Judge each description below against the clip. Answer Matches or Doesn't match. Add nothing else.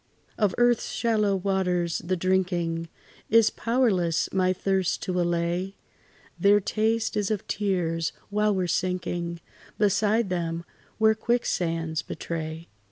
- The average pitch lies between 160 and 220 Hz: Matches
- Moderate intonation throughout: Matches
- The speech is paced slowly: Matches